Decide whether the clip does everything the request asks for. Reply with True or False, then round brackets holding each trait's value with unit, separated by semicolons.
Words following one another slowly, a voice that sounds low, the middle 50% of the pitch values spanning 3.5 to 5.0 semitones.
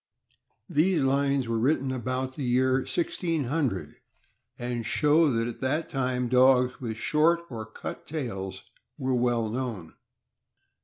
False (125 wpm; 130 Hz; 3.0 semitones)